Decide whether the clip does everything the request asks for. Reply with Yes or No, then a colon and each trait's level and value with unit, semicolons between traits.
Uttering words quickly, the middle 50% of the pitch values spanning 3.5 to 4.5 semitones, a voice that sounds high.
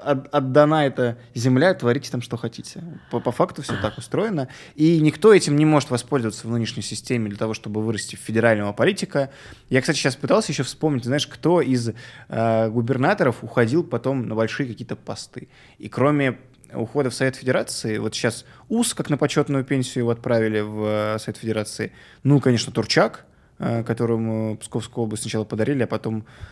No: fast, 170 wpm; average, 4.2 semitones; low, 125 Hz